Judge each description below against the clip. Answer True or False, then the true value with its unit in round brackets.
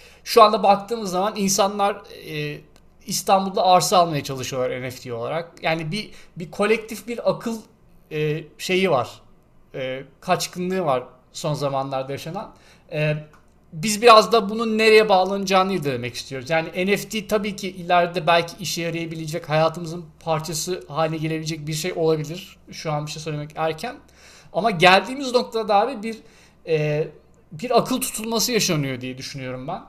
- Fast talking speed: True (145 wpm)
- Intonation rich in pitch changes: False (5.0 semitones)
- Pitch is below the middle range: False (175 Hz)